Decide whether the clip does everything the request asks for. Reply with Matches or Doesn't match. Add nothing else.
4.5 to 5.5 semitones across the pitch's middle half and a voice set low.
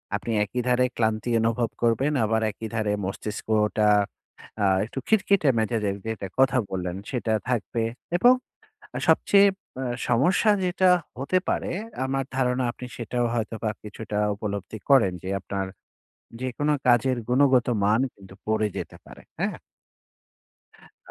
Doesn't match